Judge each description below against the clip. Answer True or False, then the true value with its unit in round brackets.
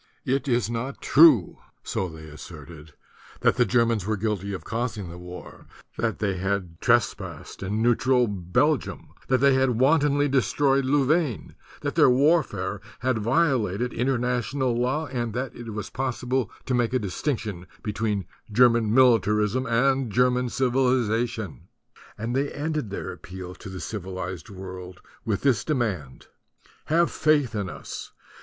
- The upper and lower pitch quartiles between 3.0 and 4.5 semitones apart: False (4.9 semitones)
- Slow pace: False (150 wpm)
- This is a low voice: True (115 Hz)